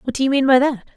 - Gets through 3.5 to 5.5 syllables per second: No, 7.0 syllables/s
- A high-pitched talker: Yes, very high, 260 Hz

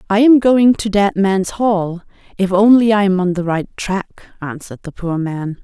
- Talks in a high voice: Yes, high, 200 Hz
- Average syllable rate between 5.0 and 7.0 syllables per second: No, 4.7 syllables/s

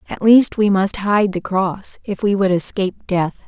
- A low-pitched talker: No, high, 195 Hz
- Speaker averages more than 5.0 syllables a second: No, 4.4 syllables/s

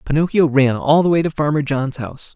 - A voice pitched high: No, medium, 145 Hz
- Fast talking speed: Yes, fast, 230 wpm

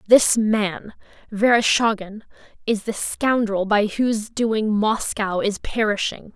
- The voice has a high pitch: Yes, high, 215 Hz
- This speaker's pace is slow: Yes, slow, 115 wpm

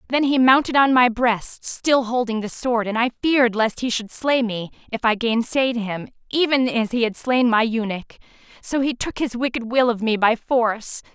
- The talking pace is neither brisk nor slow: No, fast, 210 wpm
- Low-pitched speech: No, high, 240 Hz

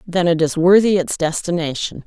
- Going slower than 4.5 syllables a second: No, 5.2 syllables/s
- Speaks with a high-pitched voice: No, medium, 170 Hz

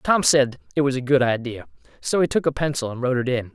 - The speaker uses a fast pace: Yes, fast, 270 wpm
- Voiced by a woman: No, male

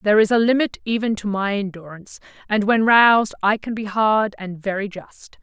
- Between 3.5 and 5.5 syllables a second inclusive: Yes, 5.3 syllables/s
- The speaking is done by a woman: Yes, female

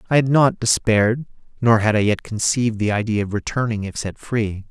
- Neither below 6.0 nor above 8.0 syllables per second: No, 5.6 syllables/s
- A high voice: No, low, 110 Hz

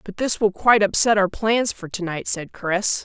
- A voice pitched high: Yes, high, 200 Hz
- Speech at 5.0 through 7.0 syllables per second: No, 4.8 syllables/s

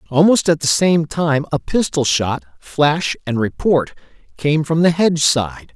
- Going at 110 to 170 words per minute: Yes, average, 165 wpm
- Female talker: No, male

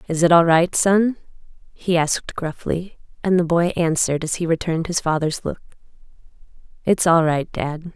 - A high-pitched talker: No, medium, 170 Hz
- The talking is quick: No, average, 150 wpm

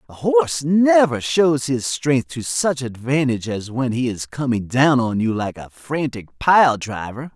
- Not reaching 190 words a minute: Yes, average, 180 wpm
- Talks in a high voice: No, low, 135 Hz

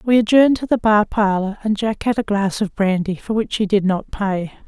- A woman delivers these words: Yes, female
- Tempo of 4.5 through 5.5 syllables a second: Yes, 5.2 syllables/s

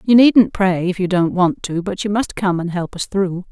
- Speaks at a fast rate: Yes, fast, 275 wpm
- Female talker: Yes, female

